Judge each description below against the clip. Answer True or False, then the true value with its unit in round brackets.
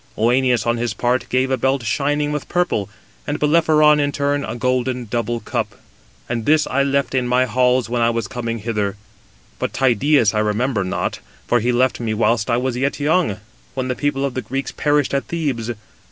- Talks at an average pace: True (195 wpm)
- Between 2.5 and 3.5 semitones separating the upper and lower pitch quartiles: True (3.1 semitones)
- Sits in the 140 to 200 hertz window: False (125 Hz)